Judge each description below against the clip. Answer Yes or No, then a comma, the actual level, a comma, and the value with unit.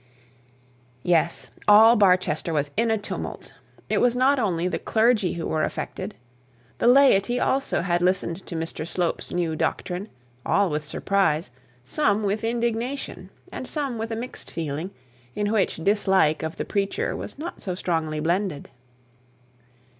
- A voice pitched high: Yes, high, 195 Hz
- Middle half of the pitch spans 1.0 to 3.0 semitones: No, average, 5.3 semitones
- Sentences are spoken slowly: No, average, 145 wpm